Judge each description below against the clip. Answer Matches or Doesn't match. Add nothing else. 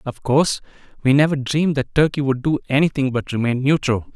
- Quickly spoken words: Doesn't match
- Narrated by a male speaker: Matches